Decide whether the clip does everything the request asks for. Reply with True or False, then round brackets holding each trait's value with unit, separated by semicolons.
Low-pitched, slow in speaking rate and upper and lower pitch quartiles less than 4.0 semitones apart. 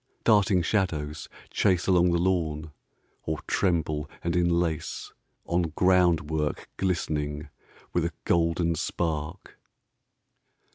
True (85 Hz; 85 wpm; 2.5 semitones)